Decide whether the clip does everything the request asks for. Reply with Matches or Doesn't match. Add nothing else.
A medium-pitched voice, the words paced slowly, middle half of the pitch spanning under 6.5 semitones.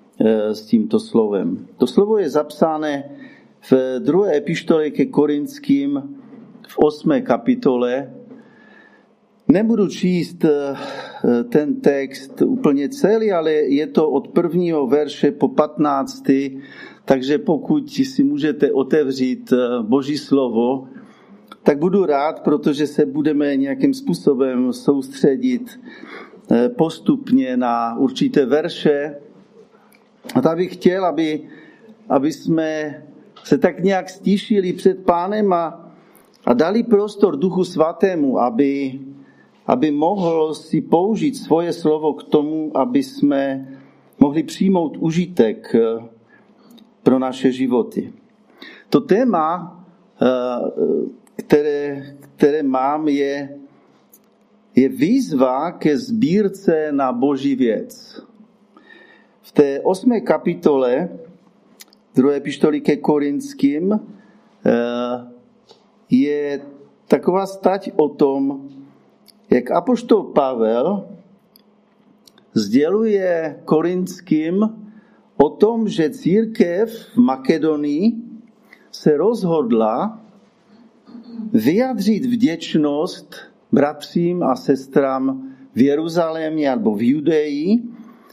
Doesn't match